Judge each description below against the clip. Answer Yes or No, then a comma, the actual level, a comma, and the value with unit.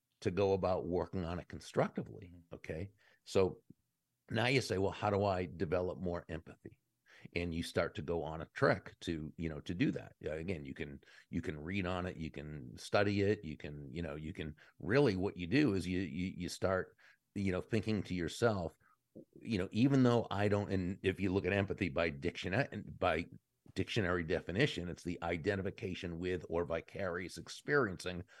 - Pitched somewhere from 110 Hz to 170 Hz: No, very low, 90 Hz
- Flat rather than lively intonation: No, average, 3.0 semitones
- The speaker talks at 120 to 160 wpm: No, average, 190 wpm